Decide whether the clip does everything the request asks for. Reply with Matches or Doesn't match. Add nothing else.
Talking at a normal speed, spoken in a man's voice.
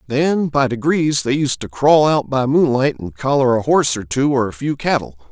Doesn't match